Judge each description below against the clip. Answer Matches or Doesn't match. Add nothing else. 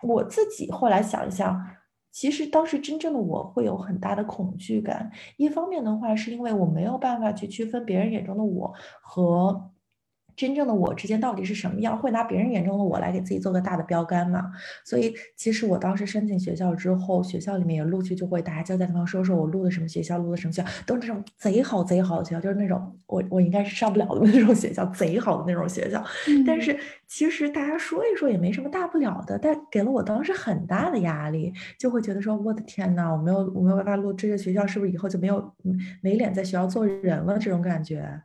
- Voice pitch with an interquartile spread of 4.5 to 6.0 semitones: Doesn't match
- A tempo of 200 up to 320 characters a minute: Doesn't match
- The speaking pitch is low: Doesn't match